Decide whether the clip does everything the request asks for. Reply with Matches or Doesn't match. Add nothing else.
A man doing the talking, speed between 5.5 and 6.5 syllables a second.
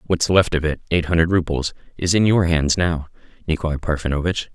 Matches